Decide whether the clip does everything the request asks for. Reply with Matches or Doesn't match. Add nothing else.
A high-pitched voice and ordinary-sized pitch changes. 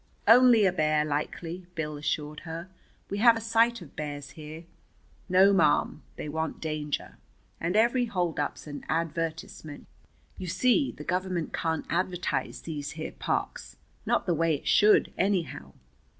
Doesn't match